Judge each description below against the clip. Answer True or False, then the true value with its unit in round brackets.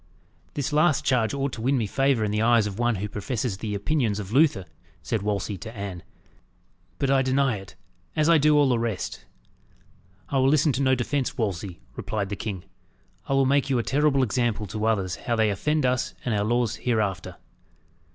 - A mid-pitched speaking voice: False (120 Hz)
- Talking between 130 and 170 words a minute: False (200 wpm)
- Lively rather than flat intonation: False (4.7 semitones)